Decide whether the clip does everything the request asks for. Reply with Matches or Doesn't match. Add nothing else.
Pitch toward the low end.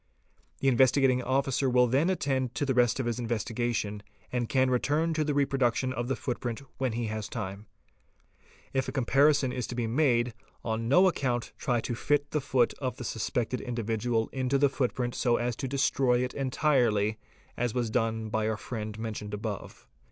Matches